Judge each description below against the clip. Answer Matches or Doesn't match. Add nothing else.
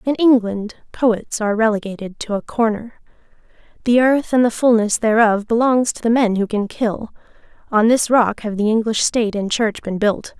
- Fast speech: Doesn't match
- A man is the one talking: Doesn't match